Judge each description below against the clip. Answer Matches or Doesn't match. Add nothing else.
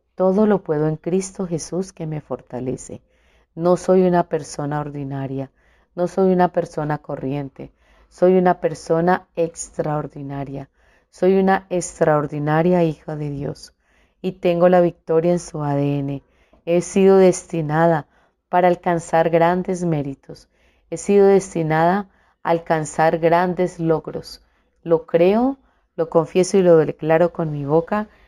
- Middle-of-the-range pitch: Matches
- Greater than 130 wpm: Doesn't match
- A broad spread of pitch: Doesn't match